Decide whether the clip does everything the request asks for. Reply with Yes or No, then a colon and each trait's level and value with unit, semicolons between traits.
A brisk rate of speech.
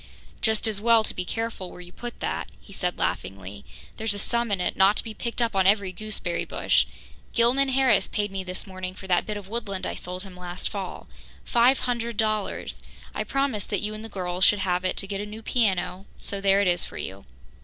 Yes: fast, 230 wpm